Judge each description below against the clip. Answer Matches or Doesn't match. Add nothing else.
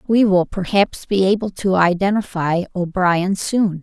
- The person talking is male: Doesn't match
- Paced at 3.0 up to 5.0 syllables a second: Matches